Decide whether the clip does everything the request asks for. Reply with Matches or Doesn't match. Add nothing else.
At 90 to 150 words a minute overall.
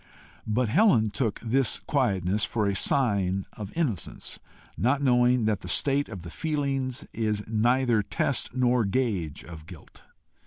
Matches